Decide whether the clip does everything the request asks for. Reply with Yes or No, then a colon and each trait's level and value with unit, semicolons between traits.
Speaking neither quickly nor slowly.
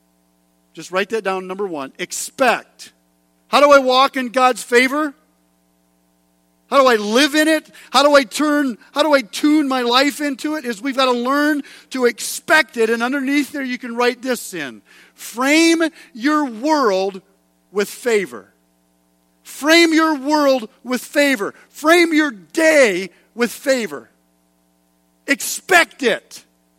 Yes: average, 145 wpm